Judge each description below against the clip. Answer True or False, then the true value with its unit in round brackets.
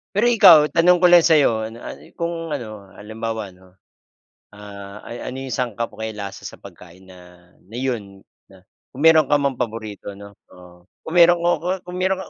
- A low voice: True (115 Hz)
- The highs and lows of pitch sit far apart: True (8.4 semitones)